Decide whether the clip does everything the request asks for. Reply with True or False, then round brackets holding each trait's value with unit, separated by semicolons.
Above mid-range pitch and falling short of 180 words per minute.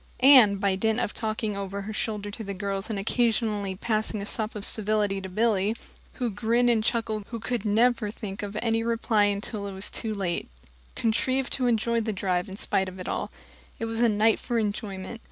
False (215 Hz; 200 wpm)